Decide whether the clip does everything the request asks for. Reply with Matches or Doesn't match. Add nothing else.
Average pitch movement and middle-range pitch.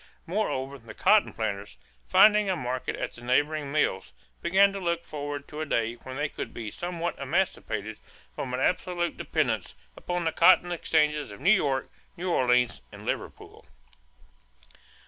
Doesn't match